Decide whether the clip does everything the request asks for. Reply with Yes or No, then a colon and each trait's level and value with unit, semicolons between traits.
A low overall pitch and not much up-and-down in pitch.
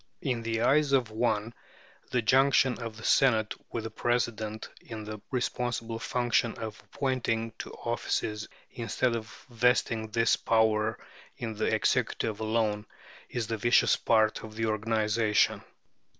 Yes: low, 115 Hz; narrow, 1.8 semitones